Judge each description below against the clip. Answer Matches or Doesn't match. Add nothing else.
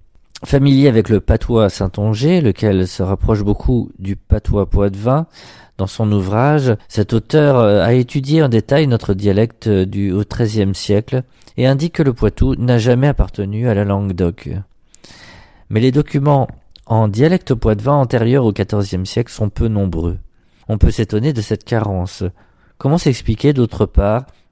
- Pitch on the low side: Matches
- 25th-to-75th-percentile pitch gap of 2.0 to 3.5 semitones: Doesn't match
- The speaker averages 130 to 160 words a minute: Matches